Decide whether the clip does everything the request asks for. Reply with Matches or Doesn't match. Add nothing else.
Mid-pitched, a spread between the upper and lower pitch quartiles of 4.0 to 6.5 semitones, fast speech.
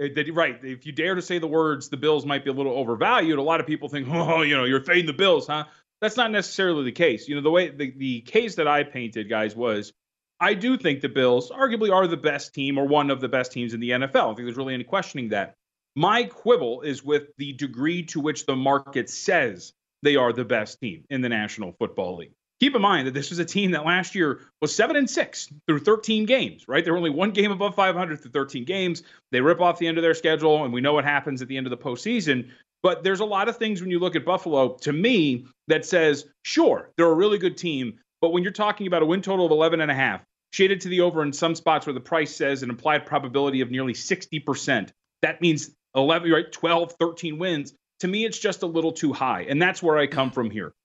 Matches